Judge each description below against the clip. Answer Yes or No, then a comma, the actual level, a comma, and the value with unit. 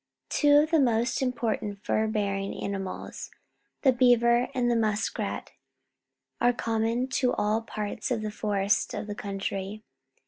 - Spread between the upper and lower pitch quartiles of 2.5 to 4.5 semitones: Yes, average, 2.9 semitones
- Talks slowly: No, average, 160 wpm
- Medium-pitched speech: No, high, 220 Hz